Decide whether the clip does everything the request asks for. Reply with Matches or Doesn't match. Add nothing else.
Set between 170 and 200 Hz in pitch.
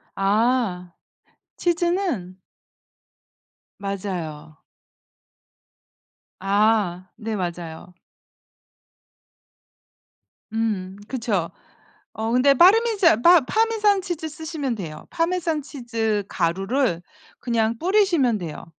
Doesn't match